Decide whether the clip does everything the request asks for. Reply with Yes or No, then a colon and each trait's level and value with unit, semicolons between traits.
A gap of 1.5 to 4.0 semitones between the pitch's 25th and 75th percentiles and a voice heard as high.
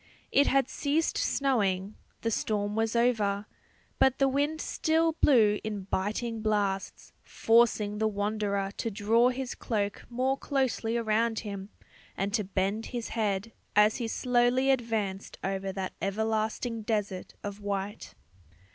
Yes: average, 3.1 semitones; high, 220 Hz